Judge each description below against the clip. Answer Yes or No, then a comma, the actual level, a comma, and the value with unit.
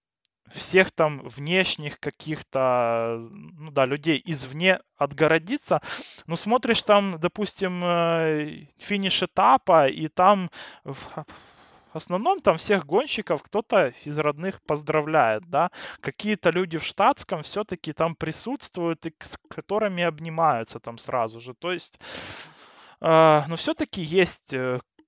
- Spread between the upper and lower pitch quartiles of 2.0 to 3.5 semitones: No, average, 4.0 semitones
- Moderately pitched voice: Yes, medium, 165 Hz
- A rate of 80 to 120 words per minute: Yes, slow, 110 wpm